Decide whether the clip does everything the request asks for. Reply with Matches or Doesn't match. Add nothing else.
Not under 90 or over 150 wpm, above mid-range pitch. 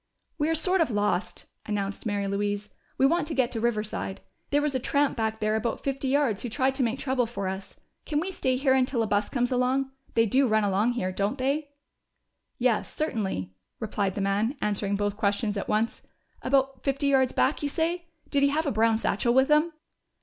Doesn't match